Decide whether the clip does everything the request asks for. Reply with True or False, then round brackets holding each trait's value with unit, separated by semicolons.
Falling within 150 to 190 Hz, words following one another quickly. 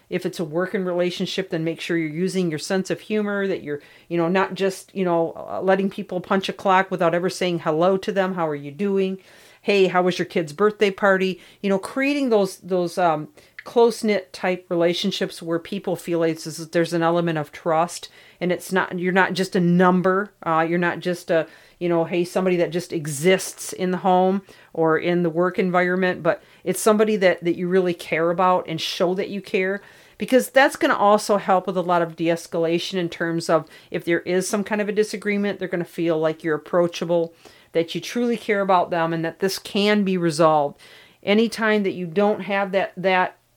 True (185 Hz; 210 wpm)